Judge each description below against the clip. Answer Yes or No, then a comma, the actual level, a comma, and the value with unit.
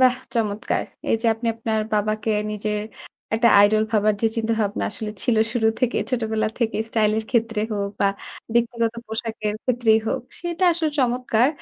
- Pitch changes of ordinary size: No, narrow, 1.9 semitones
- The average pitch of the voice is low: No, high, 225 Hz